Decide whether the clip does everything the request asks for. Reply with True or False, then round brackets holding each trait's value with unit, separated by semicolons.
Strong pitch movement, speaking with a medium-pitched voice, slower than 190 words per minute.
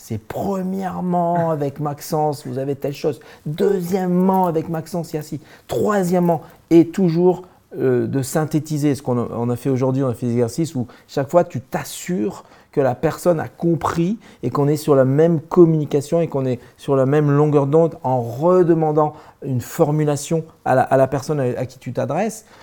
False (4.2 semitones; 150 Hz; 180 wpm)